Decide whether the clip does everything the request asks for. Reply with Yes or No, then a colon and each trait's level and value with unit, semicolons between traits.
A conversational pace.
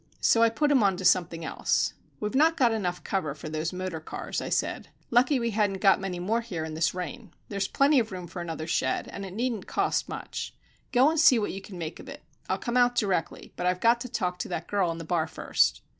No: fast, 245 wpm